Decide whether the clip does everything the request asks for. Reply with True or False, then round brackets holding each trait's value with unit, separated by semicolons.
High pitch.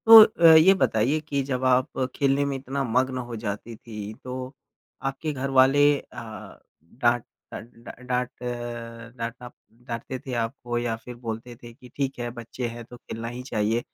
False (125 Hz)